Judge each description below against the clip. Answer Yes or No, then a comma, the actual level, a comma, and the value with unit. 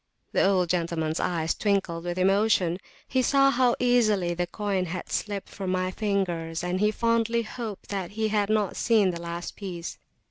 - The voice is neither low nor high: No, high, 195 Hz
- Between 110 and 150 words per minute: No, average, 175 wpm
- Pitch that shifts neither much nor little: Yes, average, 3.7 semitones